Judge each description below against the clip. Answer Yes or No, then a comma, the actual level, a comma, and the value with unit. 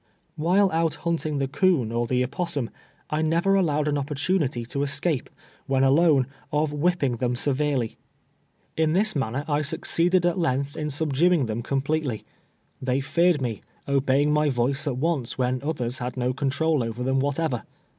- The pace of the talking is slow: No, average, 165 wpm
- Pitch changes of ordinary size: Yes, average, 3.8 semitones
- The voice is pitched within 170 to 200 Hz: No, medium, 145 Hz